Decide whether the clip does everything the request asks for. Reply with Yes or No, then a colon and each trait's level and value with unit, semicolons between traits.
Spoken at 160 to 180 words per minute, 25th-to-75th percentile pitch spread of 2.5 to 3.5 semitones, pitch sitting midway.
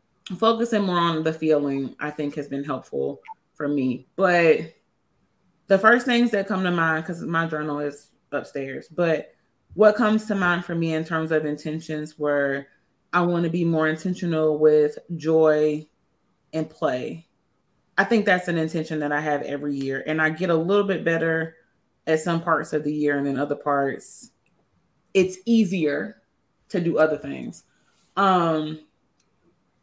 Yes: average, 165 wpm; average, 3.0 semitones; medium, 160 Hz